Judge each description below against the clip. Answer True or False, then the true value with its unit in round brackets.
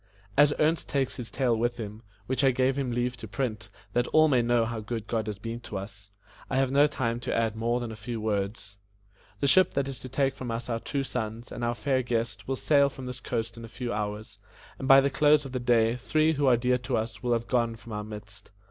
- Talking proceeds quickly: True (255 wpm)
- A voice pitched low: True (120 Hz)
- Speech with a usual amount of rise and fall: True (3.0 semitones)